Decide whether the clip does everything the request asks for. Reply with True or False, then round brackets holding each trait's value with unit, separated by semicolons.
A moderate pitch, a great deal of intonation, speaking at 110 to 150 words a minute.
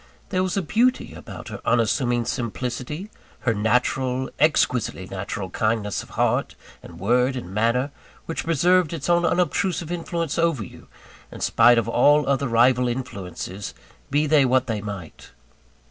False (125 Hz; 5.8 semitones; 145 wpm)